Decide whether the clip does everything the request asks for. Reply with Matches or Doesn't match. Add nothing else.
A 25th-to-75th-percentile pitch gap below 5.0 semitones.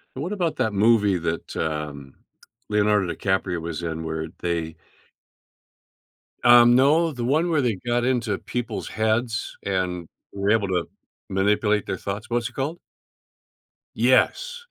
Doesn't match